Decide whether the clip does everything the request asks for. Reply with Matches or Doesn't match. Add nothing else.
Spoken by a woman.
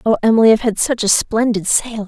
Matches